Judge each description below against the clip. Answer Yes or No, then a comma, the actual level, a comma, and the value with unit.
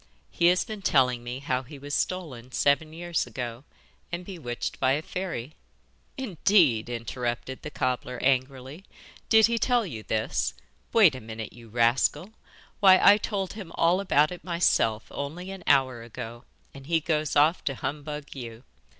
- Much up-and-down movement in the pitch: Yes, wide, 6.4 semitones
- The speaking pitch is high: No, medium, 145 Hz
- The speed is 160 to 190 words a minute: Yes, average, 165 wpm